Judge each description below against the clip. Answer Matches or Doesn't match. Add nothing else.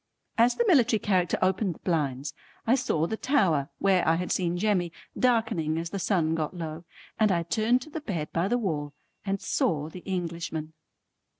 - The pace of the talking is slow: Doesn't match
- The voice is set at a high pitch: Doesn't match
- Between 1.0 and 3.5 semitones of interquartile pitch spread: Doesn't match